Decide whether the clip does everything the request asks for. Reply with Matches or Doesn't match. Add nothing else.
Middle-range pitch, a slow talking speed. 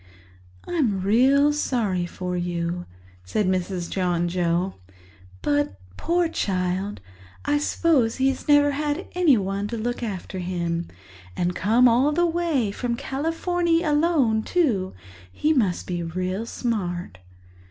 Doesn't match